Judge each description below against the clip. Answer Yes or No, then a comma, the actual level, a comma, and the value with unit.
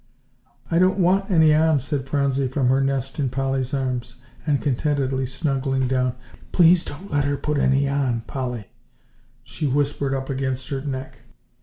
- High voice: No, low, 135 Hz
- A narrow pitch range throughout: Yes, narrow, 1.9 semitones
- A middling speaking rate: Yes, average, 160 wpm